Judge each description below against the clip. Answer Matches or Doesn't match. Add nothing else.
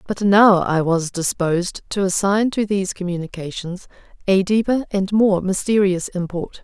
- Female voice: Matches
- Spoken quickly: Doesn't match